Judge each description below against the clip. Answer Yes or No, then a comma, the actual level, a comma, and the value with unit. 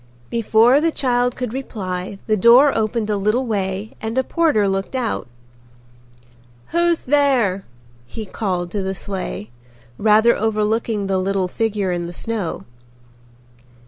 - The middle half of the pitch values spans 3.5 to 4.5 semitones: Yes, average, 4.0 semitones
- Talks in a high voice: Yes, high, 215 Hz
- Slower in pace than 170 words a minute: Yes, slow, 135 wpm